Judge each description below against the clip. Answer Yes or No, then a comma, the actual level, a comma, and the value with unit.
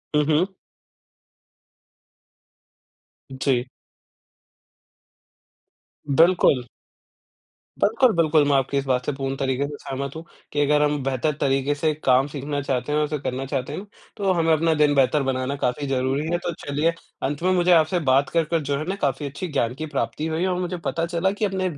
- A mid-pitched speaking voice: Yes, medium, 145 Hz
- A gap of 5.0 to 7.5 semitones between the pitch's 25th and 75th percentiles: No, average, 3.5 semitones